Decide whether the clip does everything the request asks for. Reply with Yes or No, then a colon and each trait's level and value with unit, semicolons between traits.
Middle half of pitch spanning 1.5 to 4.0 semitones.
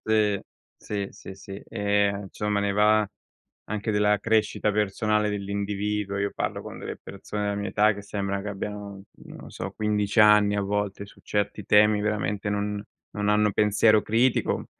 No: narrow, 0.8 semitones